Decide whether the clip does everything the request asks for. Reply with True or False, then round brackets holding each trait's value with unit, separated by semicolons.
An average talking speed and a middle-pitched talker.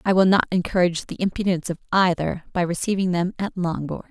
True (190 wpm; 180 Hz)